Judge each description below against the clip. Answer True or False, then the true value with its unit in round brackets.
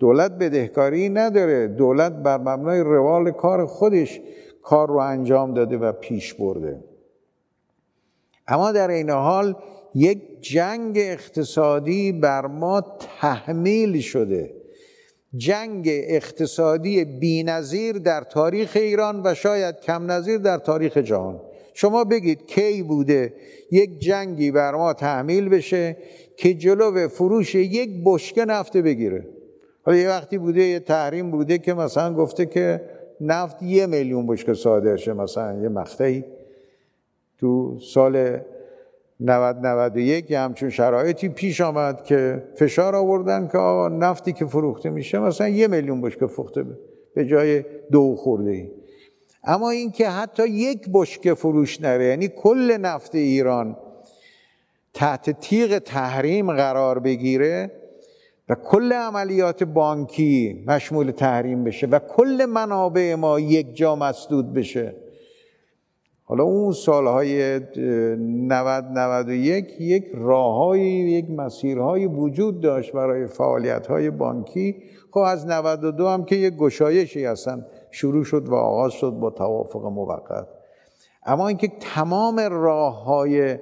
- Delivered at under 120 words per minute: False (125 wpm)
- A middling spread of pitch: False (6.4 semitones)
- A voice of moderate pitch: True (160 Hz)